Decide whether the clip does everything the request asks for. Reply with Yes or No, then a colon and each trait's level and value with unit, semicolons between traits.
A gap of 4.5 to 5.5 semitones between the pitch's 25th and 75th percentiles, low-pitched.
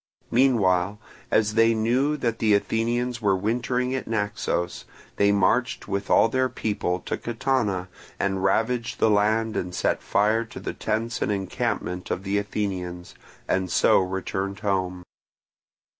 No: average, 3.3 semitones; low, 105 Hz